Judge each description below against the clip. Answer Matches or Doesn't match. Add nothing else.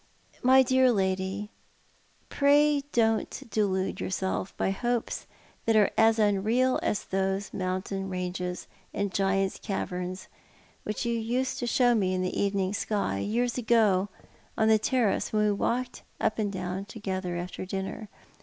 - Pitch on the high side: Matches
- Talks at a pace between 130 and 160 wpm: Matches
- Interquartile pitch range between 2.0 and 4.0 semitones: Matches